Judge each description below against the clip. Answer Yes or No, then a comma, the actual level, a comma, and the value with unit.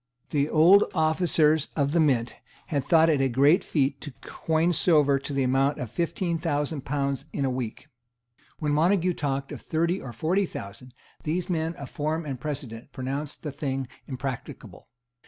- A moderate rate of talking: Yes, average, 170 wpm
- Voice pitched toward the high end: No, medium, 145 Hz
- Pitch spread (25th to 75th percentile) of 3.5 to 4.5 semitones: No, average, 3.1 semitones